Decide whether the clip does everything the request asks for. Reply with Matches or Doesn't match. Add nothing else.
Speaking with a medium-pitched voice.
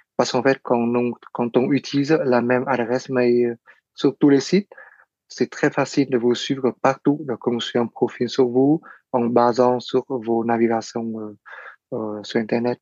Doesn't match